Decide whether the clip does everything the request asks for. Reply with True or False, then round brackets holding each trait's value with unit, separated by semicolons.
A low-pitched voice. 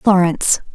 False (185 Hz)